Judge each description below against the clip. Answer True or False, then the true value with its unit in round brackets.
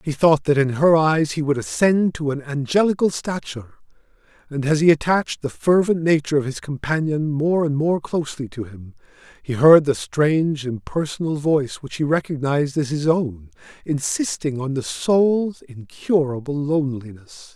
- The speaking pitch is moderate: True (145 Hz)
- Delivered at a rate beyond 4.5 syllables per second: True (5.0 syllables/s)